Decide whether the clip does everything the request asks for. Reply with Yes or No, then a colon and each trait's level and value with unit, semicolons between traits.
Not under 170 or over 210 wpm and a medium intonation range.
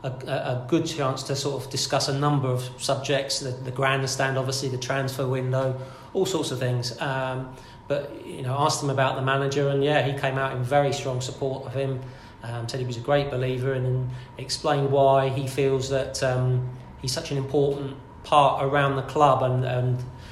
No: average, 200 wpm; narrow, 1.3 semitones